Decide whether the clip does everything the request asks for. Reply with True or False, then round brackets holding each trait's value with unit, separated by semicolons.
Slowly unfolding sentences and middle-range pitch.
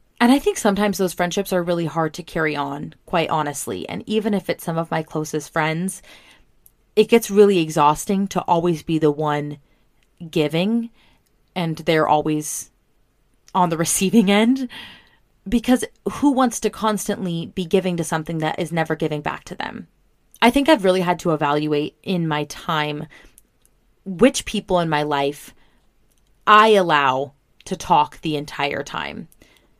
False (155 wpm; 175 Hz)